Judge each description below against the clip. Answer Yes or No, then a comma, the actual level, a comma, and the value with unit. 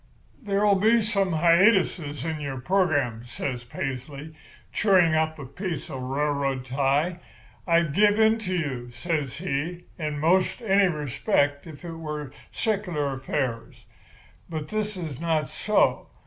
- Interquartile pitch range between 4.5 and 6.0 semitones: Yes, average, 5.0 semitones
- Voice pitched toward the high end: No, medium, 155 Hz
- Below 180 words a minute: Yes, average, 140 wpm